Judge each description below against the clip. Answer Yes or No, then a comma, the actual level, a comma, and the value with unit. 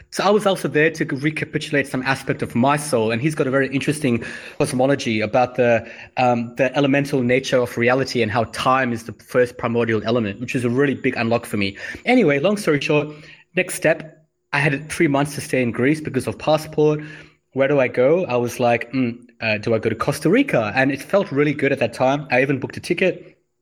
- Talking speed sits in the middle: No, fast, 225 wpm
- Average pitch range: Yes, average, 4.0 semitones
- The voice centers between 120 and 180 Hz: Yes, low, 135 Hz